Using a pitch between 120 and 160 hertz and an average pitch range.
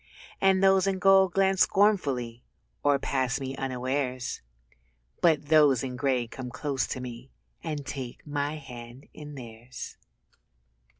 Yes: low, 135 Hz; average, 3.9 semitones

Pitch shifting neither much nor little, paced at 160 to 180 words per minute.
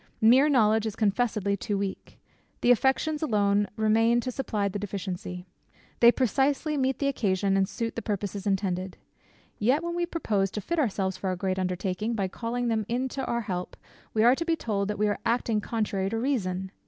No: average, 4.0 semitones; average, 190 wpm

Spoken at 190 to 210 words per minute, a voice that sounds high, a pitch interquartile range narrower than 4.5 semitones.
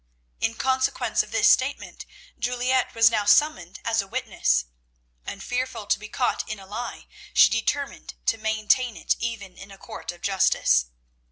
No: average, 165 wpm; high, 225 Hz; average, 3.8 semitones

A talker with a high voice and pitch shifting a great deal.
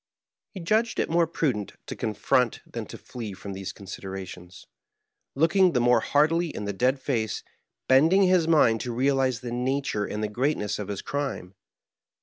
No: low, 125 Hz; wide, 6.7 semitones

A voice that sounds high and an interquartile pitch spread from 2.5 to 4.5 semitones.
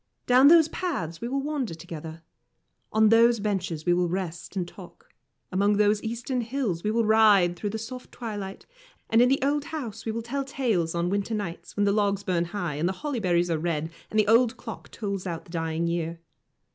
No: high, 205 Hz; average, 5.2 semitones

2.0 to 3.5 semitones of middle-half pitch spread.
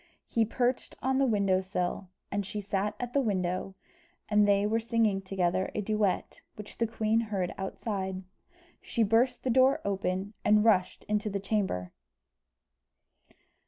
Yes: average, 2.8 semitones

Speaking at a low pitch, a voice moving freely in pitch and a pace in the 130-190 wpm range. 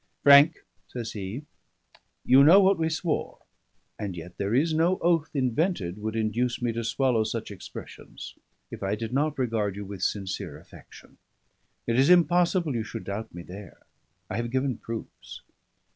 Yes: low, 120 Hz; wide, 6.5 semitones; average, 160 wpm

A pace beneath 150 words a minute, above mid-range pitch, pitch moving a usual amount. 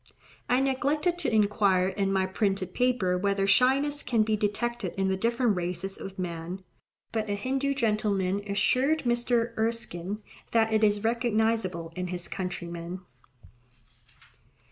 Yes: slow, 135 wpm; high, 210 Hz; average, 4.1 semitones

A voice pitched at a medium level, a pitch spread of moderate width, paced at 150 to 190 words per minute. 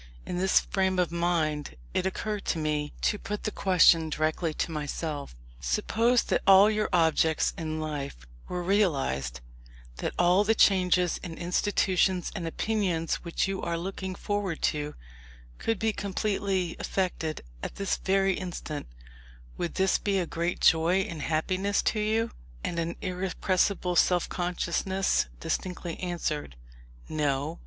No: medium, 180 Hz; average, 3.3 semitones; average, 140 wpm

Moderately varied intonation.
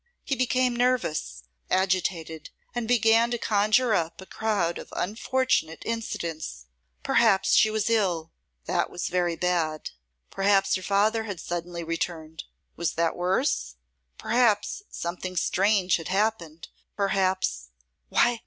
Yes: average, 4.8 semitones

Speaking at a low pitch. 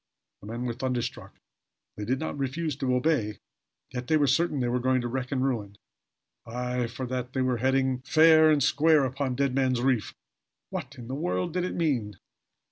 Yes: low, 130 Hz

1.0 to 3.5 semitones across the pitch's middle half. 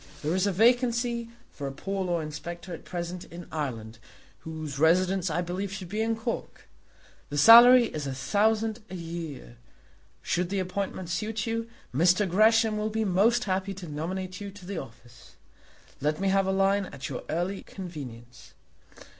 No: average, 4.7 semitones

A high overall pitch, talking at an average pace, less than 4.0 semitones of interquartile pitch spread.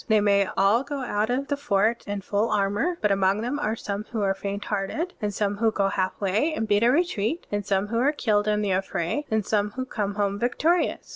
No: high, 210 Hz; fast, 225 wpm; average, 3.5 semitones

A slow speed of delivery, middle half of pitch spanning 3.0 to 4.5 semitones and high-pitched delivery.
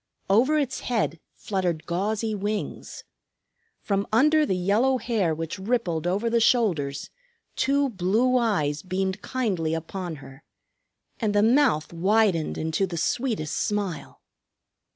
No: slow, 125 wpm; wide, 5.5 semitones; high, 200 Hz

